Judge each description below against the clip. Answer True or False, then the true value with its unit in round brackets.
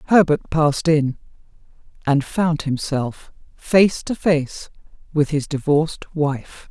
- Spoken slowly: True (105 wpm)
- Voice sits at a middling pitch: True (155 Hz)